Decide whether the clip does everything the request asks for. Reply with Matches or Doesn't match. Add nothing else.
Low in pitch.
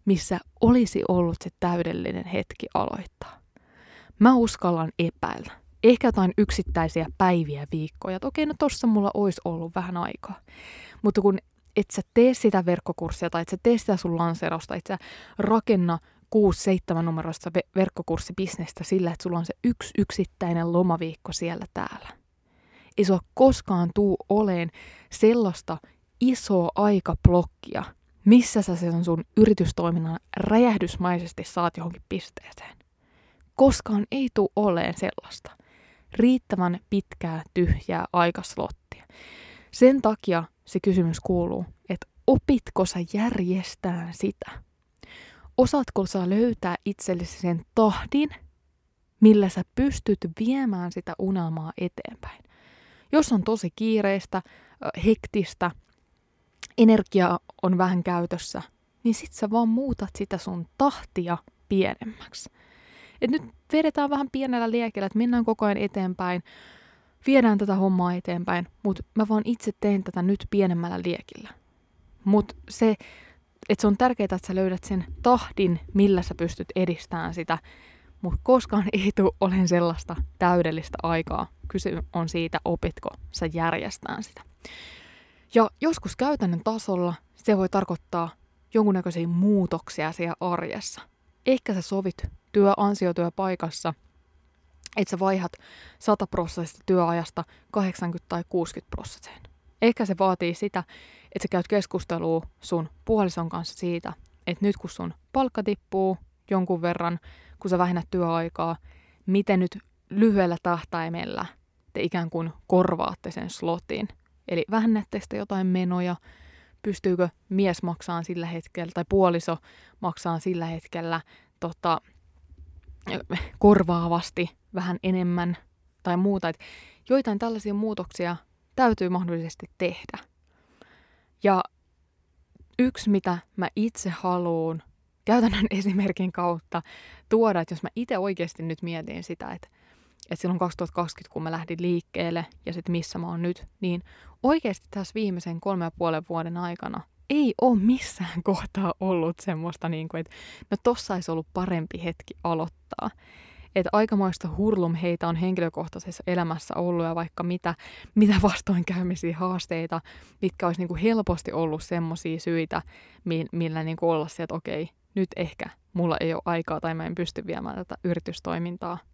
Doesn't match